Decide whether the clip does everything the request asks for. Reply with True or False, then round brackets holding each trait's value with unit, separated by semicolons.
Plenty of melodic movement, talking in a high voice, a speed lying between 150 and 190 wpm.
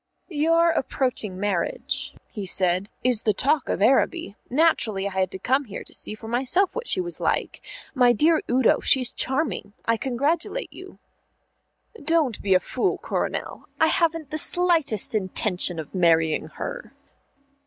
True (8.2 semitones; 250 Hz; 155 wpm)